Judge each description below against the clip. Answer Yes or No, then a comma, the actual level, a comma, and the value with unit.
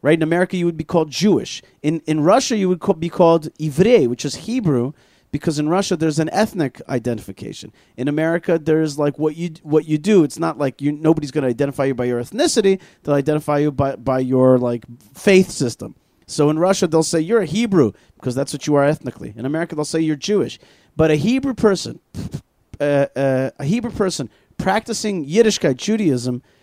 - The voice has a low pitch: No, medium, 155 Hz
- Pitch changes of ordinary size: Yes, average, 4.5 semitones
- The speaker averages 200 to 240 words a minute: Yes, fast, 205 wpm